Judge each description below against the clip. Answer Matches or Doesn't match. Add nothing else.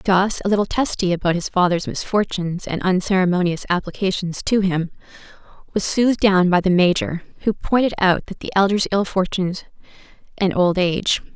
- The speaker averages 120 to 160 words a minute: Matches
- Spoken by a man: Doesn't match